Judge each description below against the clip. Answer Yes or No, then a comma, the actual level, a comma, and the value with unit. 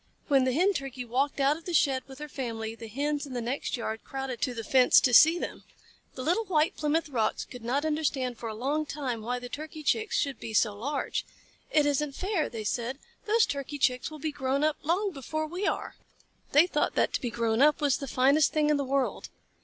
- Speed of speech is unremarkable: No, fast, 230 wpm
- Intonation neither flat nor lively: Yes, average, 3.5 semitones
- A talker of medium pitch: No, very high, 275 Hz